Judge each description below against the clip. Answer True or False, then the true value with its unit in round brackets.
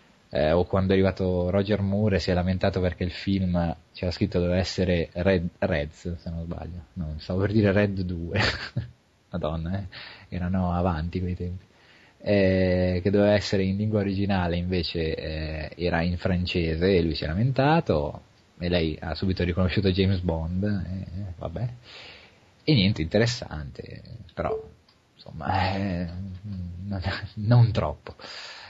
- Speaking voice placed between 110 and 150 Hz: False (95 Hz)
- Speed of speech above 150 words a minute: False (145 wpm)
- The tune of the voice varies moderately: False (2.2 semitones)